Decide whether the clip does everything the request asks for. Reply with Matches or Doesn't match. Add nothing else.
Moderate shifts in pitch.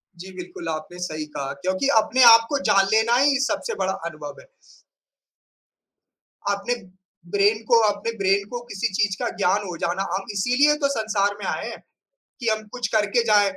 Matches